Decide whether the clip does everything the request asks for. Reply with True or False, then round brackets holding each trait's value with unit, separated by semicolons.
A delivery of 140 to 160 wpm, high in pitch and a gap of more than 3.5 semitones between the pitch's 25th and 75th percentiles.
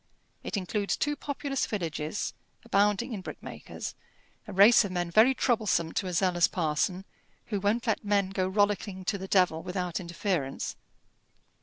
False (150 wpm; 195 Hz; 2.8 semitones)